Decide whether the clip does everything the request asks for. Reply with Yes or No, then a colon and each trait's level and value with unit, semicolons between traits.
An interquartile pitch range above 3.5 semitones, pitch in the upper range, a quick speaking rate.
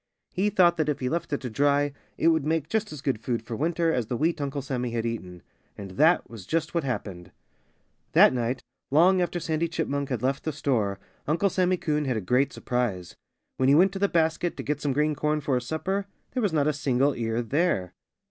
No: average, 4.9 semitones; medium, 145 Hz; fast, 225 wpm